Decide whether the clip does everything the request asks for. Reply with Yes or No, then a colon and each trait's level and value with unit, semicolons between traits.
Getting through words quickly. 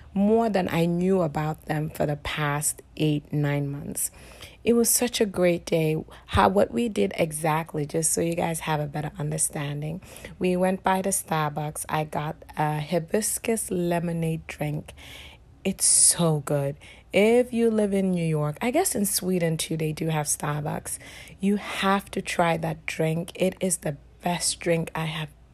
No: average, 170 wpm